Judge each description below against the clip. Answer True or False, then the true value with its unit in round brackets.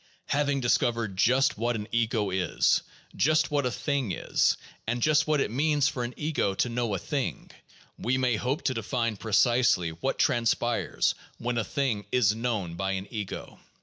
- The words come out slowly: False (175 wpm)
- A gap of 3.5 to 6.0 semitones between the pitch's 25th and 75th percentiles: True (4.2 semitones)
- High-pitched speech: False (120 Hz)